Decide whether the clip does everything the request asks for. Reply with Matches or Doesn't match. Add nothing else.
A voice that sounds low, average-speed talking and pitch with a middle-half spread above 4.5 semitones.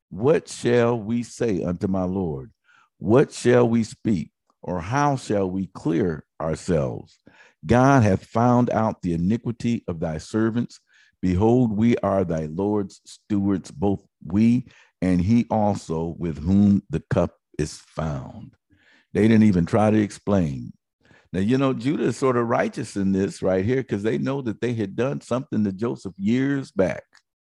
Doesn't match